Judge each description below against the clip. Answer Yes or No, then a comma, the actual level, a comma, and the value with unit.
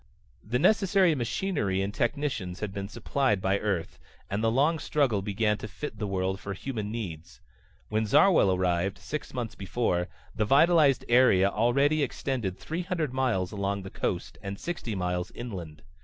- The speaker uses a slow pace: No, average, 160 wpm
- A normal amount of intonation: No, wide, 6.1 semitones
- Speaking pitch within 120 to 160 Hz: No, low, 110 Hz